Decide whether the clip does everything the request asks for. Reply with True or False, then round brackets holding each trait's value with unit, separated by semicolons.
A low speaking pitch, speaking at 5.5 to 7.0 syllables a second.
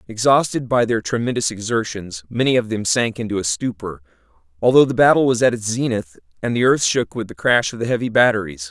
True (110 Hz; 5.9 syllables/s)